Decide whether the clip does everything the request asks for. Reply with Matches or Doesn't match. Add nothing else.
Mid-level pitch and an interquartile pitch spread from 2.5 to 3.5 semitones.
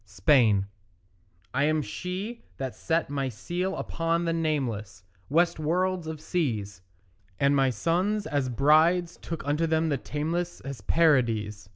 Doesn't match